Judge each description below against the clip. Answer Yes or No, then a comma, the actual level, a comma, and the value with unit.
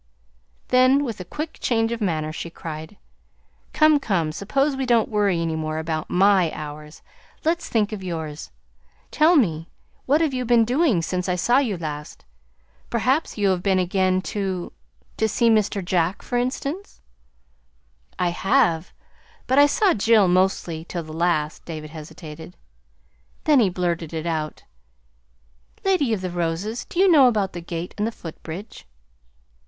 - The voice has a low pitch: No, high, 190 Hz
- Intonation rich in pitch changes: Yes, wide, 6.6 semitones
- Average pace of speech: Yes, average, 160 wpm